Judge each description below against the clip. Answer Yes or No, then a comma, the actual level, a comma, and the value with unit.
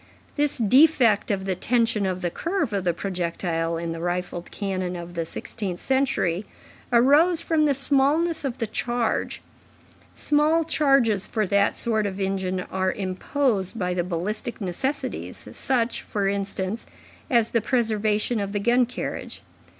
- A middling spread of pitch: No, wide, 5.8 semitones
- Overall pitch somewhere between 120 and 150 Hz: No, high, 210 Hz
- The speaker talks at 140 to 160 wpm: Yes, average, 150 wpm